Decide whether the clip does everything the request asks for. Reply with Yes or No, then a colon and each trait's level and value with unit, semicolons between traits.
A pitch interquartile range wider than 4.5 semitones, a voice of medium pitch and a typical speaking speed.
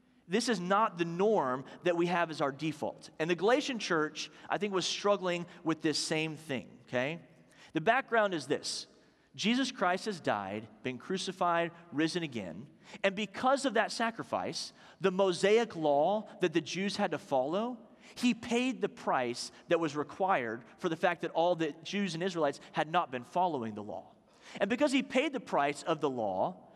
Yes: average, 5.2 semitones; medium, 180 Hz; average, 180 wpm